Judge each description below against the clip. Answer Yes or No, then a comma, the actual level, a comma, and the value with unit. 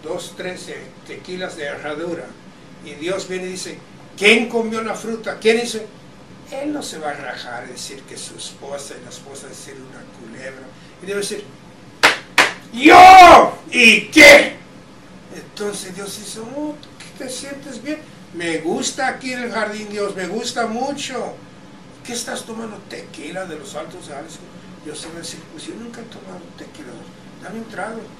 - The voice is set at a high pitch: Yes, high, 210 Hz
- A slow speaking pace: No, average, 170 wpm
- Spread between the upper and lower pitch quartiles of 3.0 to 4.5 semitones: No, average, 5.3 semitones